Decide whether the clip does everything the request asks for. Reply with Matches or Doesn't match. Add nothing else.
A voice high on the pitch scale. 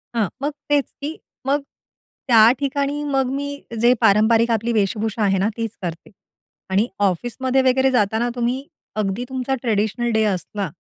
Matches